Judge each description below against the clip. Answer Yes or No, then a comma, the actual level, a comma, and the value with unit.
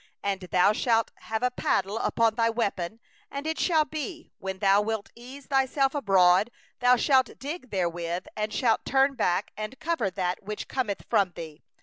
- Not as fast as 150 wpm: No, average, 165 wpm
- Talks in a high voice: Yes, high, 225 Hz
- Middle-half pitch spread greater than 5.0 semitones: Yes, wide, 5.5 semitones